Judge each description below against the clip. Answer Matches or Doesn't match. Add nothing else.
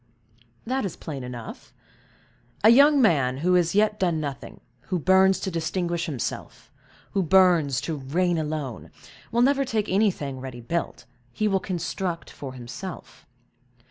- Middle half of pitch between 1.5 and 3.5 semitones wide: Doesn't match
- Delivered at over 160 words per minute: Doesn't match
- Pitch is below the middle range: Doesn't match